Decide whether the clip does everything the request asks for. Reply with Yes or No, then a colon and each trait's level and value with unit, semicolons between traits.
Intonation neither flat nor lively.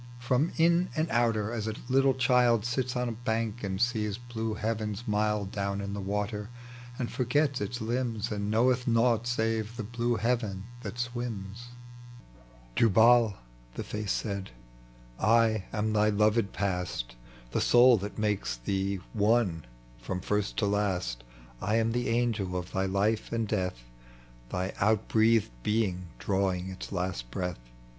Yes: average, 3.3 semitones